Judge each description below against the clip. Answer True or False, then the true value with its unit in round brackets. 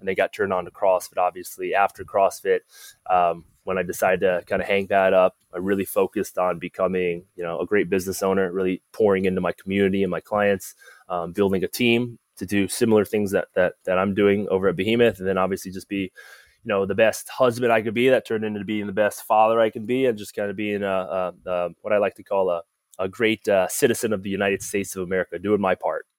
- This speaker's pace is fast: True (240 wpm)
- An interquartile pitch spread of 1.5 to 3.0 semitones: True (2.7 semitones)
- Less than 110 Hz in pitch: True (100 Hz)